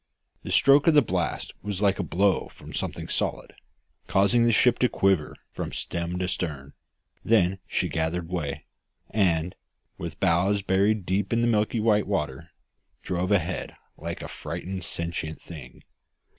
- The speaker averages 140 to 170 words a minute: Yes, average, 155 wpm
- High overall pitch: No, very low, 95 Hz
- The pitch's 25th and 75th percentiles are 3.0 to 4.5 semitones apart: Yes, average, 3.5 semitones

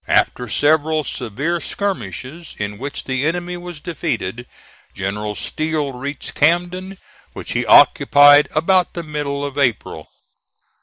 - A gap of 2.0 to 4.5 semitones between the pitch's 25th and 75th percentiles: No, average, 4.9 semitones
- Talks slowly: Yes, slow, 120 wpm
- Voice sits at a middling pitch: Yes, medium, 145 Hz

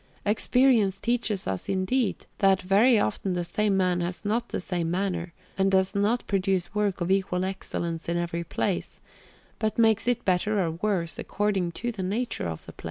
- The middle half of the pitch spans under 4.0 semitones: Yes, average, 3.1 semitones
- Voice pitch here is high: Yes, high, 195 Hz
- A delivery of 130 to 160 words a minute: No, average, 180 wpm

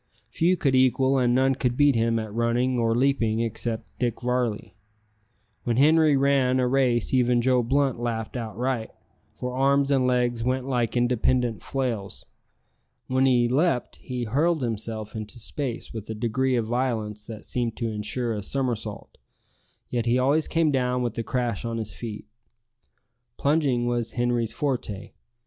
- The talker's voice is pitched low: Yes, low, 125 Hz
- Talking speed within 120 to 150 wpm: No, average, 160 wpm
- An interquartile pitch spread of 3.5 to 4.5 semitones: No, narrow, 2.4 semitones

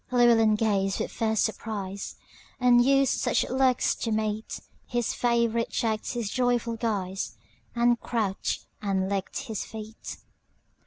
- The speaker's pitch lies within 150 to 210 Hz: No, high, 225 Hz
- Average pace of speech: No, slow, 105 wpm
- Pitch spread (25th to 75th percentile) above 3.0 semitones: No, narrow, 2.4 semitones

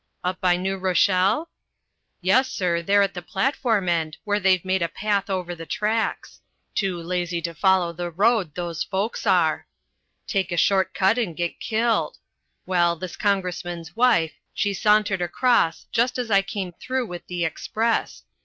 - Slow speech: No, average, 165 wpm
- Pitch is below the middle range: No, high, 190 Hz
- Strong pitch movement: No, average, 3.3 semitones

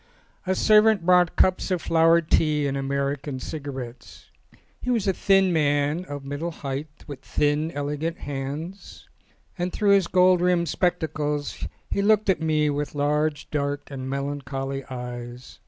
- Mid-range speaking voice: Yes, medium, 150 Hz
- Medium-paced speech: Yes, average, 150 wpm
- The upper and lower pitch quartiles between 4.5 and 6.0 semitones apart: No, average, 4.1 semitones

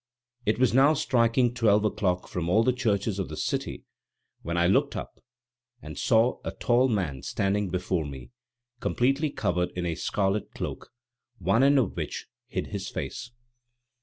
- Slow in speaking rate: No, average, 165 wpm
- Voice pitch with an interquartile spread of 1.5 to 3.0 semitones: No, average, 5.3 semitones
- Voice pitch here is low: Yes, low, 105 Hz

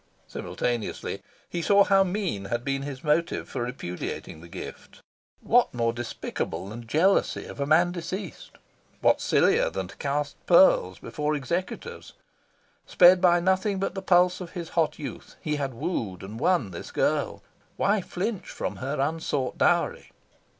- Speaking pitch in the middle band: Yes, medium, 150 Hz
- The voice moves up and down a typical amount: No, wide, 7.0 semitones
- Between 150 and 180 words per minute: Yes, average, 155 wpm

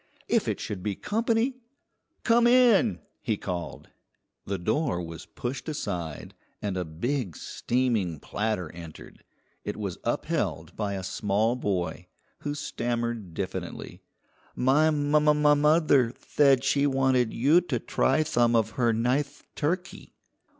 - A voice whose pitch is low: Yes, low, 120 Hz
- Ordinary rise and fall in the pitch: No, wide, 6.8 semitones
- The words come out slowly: Yes, slow, 130 wpm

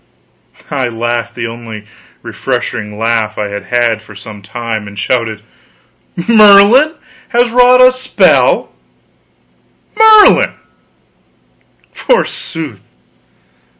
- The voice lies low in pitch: Yes, low, 120 Hz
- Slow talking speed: Yes, slow, 95 wpm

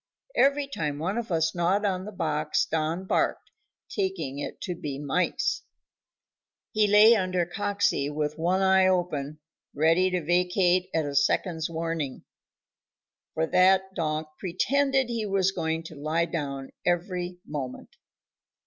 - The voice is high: No, medium, 175 Hz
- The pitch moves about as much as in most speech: Yes, average, 3.6 semitones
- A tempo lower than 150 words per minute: Yes, average, 140 wpm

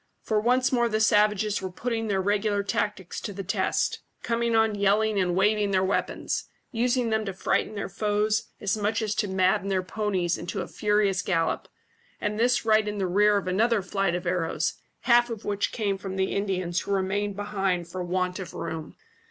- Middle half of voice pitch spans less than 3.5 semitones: Yes, narrow, 2.4 semitones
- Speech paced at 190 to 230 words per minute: Yes, average, 195 wpm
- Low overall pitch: No, high, 205 Hz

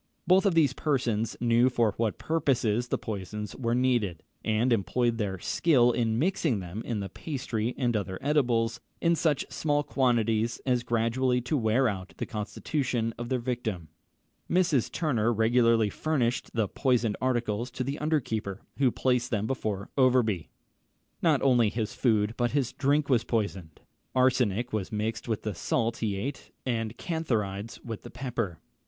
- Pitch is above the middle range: No, low, 120 Hz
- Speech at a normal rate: Yes, average, 160 wpm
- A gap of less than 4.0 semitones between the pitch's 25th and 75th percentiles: Yes, average, 3.1 semitones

